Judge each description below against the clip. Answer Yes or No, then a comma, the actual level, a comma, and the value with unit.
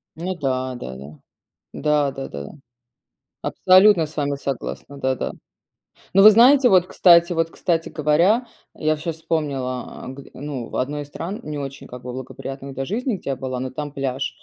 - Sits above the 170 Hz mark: No, medium, 145 Hz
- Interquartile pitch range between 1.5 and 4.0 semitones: No, average, 4.5 semitones